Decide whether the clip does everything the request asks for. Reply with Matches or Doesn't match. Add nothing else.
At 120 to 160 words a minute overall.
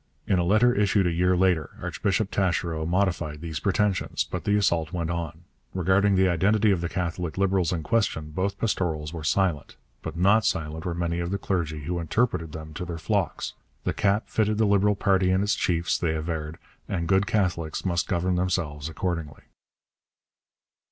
Doesn't match